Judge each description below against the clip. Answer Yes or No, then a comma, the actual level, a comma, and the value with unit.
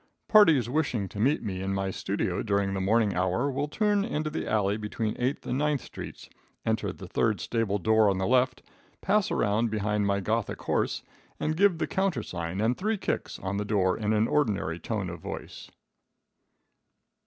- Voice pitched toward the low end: Yes, low, 110 Hz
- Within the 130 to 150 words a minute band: No, average, 180 wpm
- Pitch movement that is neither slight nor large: No, wide, 6.3 semitones